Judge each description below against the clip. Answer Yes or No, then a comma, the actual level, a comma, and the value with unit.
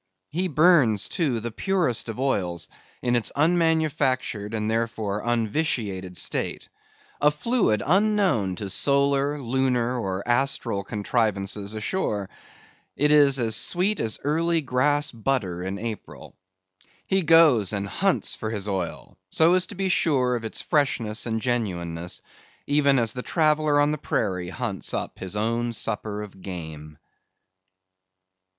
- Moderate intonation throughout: No, wide, 6.2 semitones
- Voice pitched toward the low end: Yes, low, 120 Hz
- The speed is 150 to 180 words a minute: No, slow, 135 wpm